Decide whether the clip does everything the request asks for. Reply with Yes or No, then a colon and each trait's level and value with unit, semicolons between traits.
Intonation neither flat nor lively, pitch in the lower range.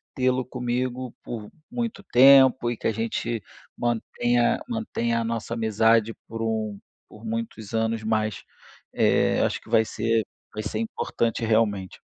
No: narrow, 1.9 semitones; low, 115 Hz